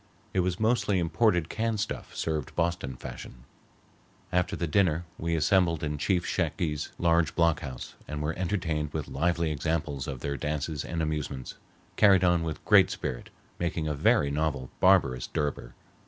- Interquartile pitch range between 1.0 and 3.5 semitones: Yes, average, 3.1 semitones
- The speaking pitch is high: No, very low, 80 Hz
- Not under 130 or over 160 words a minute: Yes, average, 155 wpm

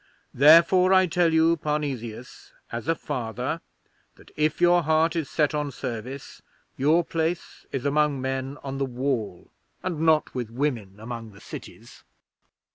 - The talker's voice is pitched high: No, medium, 145 Hz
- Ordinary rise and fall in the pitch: Yes, average, 4.4 semitones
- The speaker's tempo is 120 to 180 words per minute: Yes, average, 145 wpm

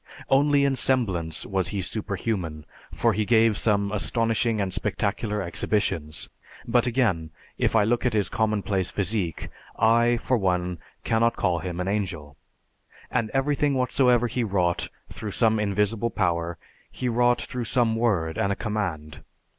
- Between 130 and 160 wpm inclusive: Yes, average, 145 wpm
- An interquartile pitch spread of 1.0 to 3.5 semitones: No, average, 4.3 semitones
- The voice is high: No, low, 105 Hz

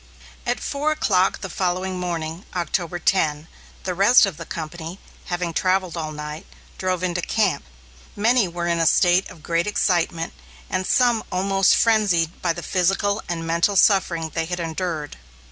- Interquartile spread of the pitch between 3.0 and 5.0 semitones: No, narrow, 2.6 semitones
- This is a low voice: No, medium, 180 Hz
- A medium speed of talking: Yes, average, 160 wpm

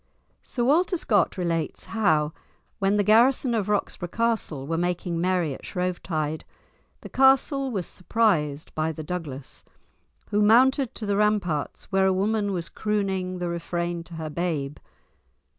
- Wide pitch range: No, average, 4.5 semitones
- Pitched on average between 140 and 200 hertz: Yes, medium, 185 Hz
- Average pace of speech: Yes, average, 145 wpm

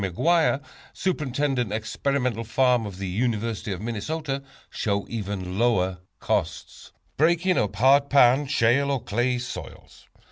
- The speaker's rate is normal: No, slow, 120 wpm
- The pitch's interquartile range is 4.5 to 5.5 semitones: Yes, average, 5.2 semitones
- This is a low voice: Yes, low, 120 Hz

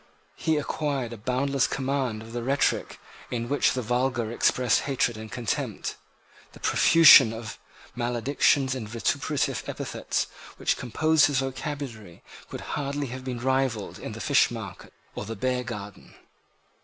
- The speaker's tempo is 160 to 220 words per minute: No, slow, 135 wpm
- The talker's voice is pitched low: Yes, low, 125 Hz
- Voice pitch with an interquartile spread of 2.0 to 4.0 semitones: Yes, average, 3.0 semitones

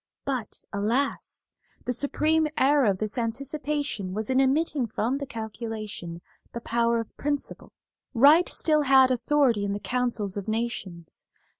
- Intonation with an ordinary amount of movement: Yes, average, 4.5 semitones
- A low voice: No, high, 240 Hz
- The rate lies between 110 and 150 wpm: Yes, average, 140 wpm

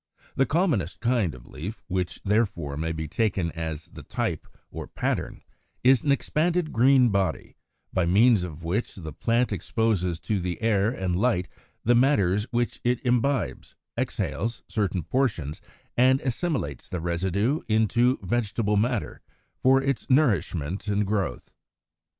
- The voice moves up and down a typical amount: No, wide, 5.7 semitones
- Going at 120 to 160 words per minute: Yes, average, 140 wpm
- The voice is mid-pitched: No, low, 105 Hz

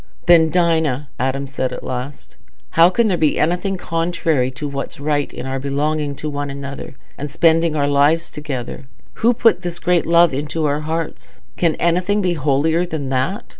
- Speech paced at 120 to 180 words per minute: Yes, average, 175 wpm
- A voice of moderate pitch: Yes, medium, 150 Hz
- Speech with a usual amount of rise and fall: Yes, average, 3.4 semitones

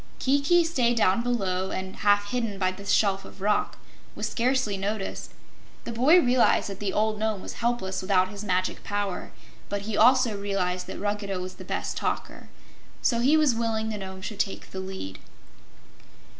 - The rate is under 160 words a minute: No, average, 175 wpm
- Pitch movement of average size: Yes, average, 3.5 semitones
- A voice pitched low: No, high, 205 Hz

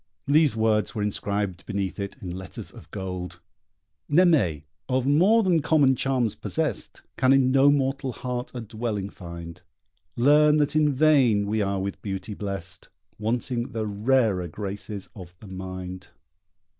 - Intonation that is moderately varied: No, wide, 5.7 semitones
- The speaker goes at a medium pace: Yes, average, 145 wpm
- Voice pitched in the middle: No, low, 110 Hz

